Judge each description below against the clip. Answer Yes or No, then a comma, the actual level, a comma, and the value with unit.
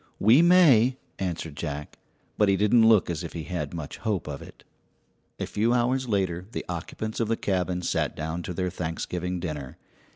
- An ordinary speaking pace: Yes, average, 185 wpm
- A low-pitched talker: Yes, very low, 90 Hz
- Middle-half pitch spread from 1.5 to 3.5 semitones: No, average, 5.1 semitones